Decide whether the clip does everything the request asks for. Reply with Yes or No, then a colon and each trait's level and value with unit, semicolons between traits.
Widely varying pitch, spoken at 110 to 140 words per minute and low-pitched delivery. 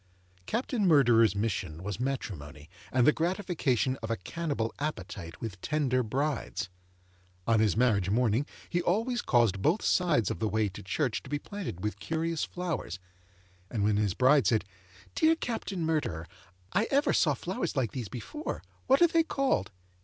No: wide, 8.2 semitones; average, 160 wpm; low, 130 Hz